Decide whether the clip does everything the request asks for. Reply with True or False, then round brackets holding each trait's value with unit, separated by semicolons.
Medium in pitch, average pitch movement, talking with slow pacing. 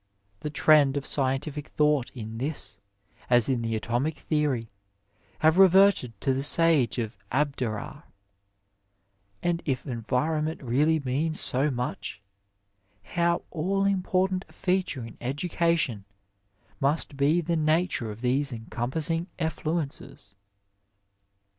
True (145 Hz; 4.8 semitones; 115 wpm)